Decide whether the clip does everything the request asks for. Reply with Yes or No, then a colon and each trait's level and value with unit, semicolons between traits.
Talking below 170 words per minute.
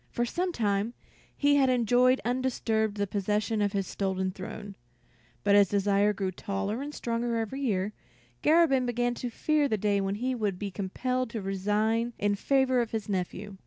No: average, 175 wpm